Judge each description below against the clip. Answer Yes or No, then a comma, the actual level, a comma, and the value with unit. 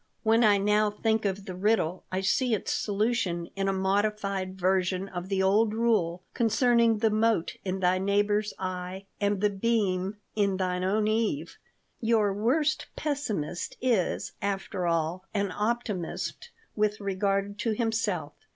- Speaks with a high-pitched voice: Yes, high, 200 Hz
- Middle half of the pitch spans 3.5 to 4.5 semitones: No, average, 2.8 semitones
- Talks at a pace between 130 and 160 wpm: Yes, average, 145 wpm